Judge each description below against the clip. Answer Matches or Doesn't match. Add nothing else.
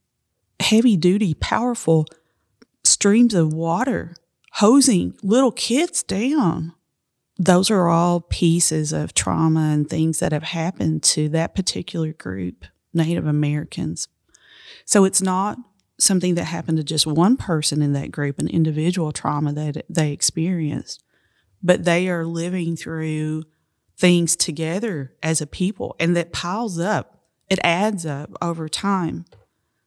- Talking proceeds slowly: Matches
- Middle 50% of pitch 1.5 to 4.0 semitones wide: Matches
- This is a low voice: Doesn't match